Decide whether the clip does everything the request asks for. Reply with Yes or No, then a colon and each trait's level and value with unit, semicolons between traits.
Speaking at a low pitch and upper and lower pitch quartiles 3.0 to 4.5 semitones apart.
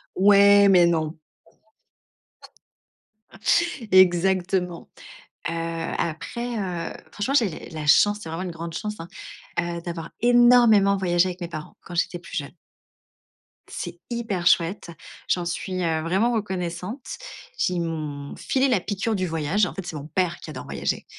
No: medium, 180 Hz; average, 3.3 semitones